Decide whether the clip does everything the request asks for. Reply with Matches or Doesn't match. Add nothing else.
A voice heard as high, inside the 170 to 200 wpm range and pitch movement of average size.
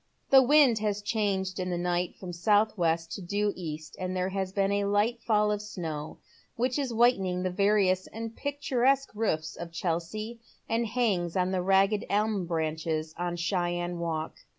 Matches